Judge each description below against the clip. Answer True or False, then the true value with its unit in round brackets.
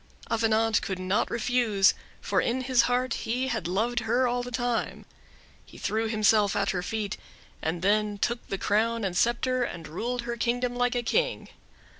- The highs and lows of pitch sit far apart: False (2.9 semitones)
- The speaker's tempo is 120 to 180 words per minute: True (175 wpm)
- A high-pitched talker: True (230 Hz)